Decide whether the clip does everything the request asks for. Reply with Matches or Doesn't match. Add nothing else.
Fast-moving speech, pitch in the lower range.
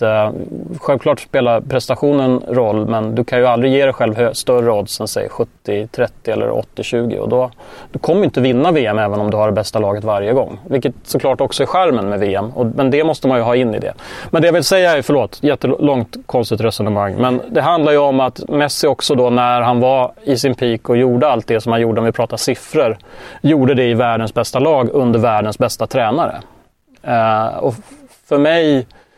Matches